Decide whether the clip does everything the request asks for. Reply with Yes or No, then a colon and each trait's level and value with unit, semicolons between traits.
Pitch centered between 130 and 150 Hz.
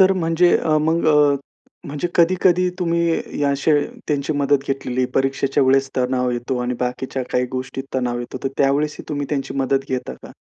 Yes: medium, 140 Hz